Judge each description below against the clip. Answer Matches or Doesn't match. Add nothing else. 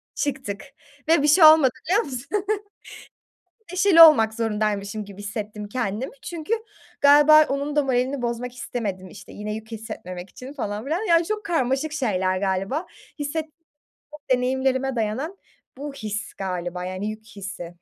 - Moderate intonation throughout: Doesn't match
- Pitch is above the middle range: Matches